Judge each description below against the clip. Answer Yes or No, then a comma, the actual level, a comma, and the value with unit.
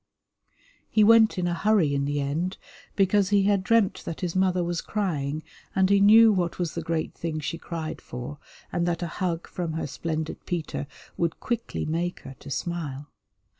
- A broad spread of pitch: No, average, 3.4 semitones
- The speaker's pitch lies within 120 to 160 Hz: No, medium, 170 Hz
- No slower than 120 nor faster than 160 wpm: No, average, 185 wpm